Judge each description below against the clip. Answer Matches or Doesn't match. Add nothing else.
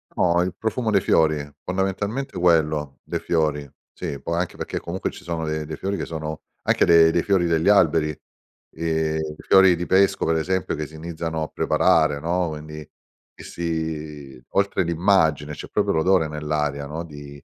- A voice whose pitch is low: Matches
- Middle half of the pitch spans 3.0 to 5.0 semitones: Doesn't match